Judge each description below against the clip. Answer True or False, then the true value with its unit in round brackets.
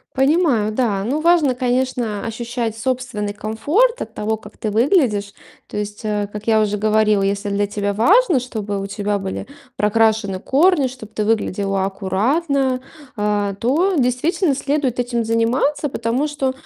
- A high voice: True (225 Hz)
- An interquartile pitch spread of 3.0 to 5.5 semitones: True (4.2 semitones)